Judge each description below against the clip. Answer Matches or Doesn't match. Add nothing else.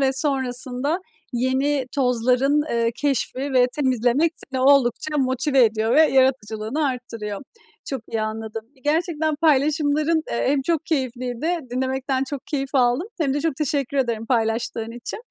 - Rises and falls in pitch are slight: Doesn't match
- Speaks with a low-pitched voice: Doesn't match